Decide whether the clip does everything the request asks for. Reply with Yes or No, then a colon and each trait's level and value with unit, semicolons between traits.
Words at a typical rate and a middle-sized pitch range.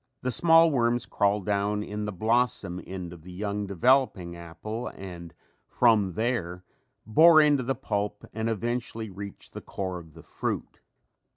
Yes: average, 155 wpm; average, 4.6 semitones